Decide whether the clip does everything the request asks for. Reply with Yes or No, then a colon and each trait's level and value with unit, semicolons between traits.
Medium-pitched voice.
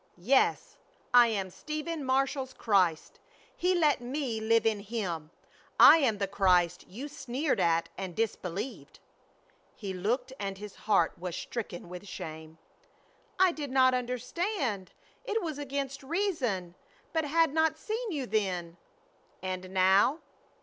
No: high, 235 Hz